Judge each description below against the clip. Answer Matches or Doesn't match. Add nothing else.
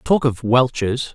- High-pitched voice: Doesn't match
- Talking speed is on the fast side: Doesn't match